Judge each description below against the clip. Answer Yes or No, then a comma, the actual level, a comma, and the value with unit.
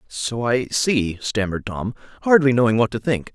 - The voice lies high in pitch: No, low, 120 Hz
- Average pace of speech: Yes, average, 180 wpm